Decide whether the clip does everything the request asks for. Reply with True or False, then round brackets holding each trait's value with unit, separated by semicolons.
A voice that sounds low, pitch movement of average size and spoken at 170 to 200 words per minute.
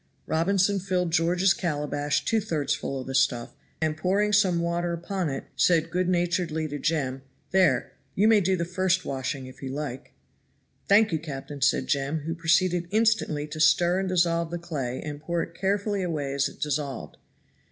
False (170 Hz; 4.0 semitones; 180 wpm)